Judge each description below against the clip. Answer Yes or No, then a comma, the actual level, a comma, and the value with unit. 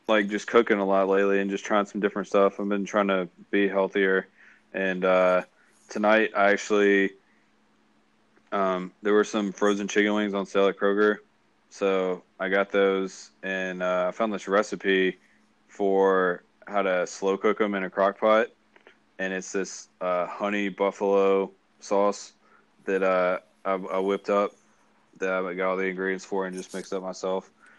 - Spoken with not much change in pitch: Yes, narrow, 1.4 semitones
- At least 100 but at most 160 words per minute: No, average, 170 wpm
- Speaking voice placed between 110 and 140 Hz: No, very low, 95 Hz